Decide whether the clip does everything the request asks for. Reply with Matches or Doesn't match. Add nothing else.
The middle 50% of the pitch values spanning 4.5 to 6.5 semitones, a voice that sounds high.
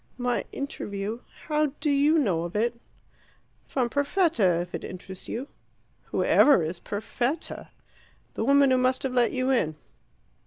Matches